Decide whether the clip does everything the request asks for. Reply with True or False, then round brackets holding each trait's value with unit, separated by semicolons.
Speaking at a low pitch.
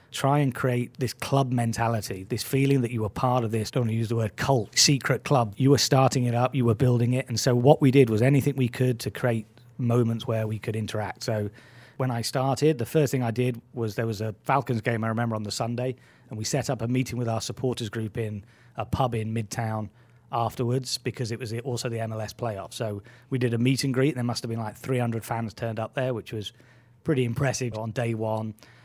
True (120 Hz)